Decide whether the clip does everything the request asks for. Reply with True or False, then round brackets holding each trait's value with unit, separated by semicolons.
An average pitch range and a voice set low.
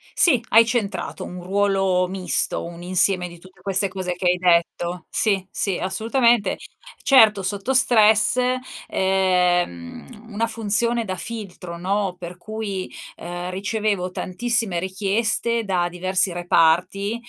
False (3.3 semitones; 190 Hz)